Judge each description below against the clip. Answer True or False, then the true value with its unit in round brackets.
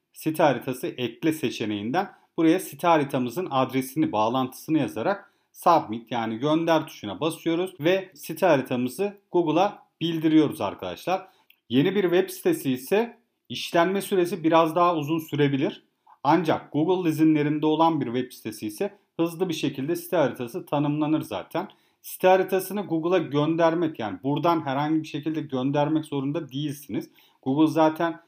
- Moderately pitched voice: True (160 Hz)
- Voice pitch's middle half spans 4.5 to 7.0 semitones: False (4.0 semitones)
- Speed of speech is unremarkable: True (130 wpm)